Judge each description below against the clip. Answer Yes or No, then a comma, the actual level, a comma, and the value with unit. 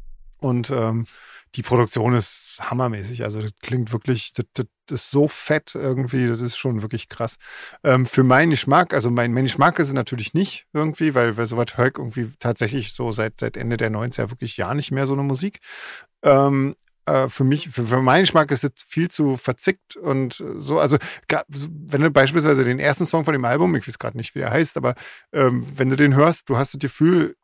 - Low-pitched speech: Yes, low, 130 Hz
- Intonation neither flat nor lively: Yes, average, 3.5 semitones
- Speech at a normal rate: No, fast, 205 wpm